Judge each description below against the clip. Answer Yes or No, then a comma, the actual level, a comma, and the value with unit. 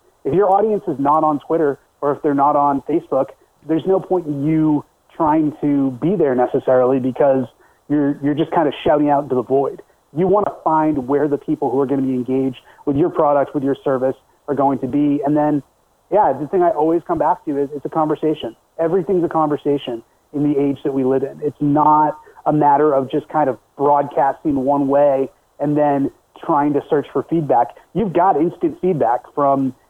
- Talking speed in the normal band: No, fast, 210 wpm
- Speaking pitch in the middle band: Yes, medium, 145 Hz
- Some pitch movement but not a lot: No, narrow, 2.0 semitones